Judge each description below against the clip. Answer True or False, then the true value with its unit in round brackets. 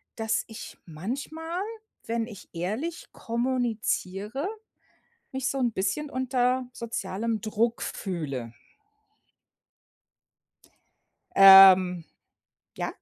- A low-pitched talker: False (225 Hz)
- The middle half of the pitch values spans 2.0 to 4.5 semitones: False (4.9 semitones)